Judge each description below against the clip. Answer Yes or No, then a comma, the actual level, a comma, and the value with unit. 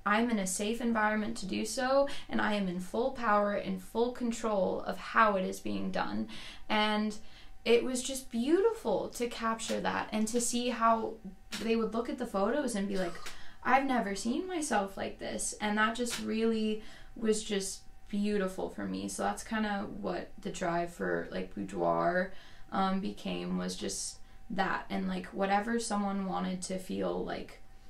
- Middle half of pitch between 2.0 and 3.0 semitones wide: No, average, 3.9 semitones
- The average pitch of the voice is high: Yes, high, 205 Hz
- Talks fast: No, average, 175 wpm